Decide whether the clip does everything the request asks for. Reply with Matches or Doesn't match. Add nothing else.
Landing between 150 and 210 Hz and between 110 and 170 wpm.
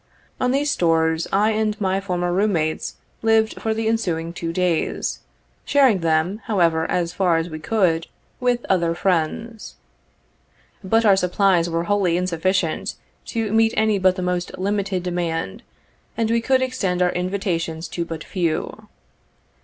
Matches